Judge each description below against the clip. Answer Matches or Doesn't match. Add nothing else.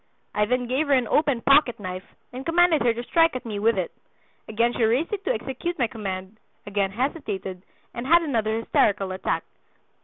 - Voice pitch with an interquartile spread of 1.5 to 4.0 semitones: Doesn't match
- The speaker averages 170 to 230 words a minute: Matches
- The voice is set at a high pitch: Matches